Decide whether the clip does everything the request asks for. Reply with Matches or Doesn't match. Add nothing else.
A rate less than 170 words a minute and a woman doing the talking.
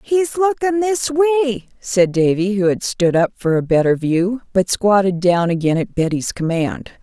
Doesn't match